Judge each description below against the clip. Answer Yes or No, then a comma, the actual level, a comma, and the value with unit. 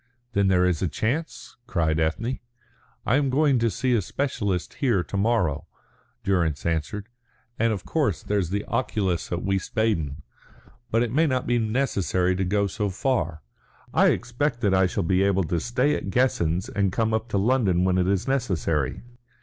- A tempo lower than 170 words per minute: No, average, 175 wpm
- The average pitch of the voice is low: Yes, low, 100 Hz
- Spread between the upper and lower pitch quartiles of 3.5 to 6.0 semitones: Yes, average, 5.0 semitones